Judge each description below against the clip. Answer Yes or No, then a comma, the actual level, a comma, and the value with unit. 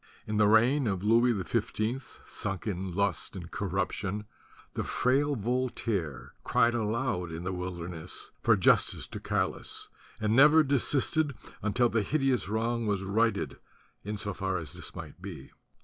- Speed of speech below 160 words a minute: Yes, average, 150 wpm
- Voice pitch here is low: Yes, low, 105 Hz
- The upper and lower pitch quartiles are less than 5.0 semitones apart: Yes, average, 4.1 semitones